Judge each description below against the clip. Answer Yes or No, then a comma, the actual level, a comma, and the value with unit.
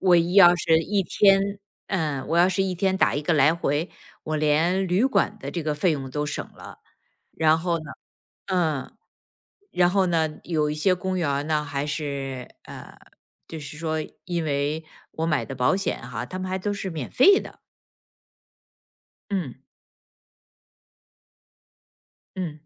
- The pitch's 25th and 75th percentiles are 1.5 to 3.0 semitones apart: No, average, 3.8 semitones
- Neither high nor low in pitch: Yes, medium, 160 Hz